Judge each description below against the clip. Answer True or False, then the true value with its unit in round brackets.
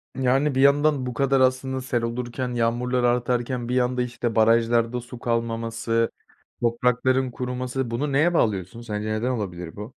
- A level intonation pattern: True (1.8 semitones)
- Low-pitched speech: True (125 Hz)